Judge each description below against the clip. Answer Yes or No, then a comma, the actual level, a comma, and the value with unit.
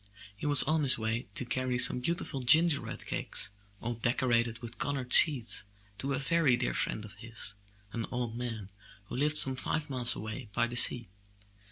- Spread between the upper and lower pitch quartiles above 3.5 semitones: No, average, 3.0 semitones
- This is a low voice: Yes, low, 125 Hz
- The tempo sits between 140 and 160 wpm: No, average, 185 wpm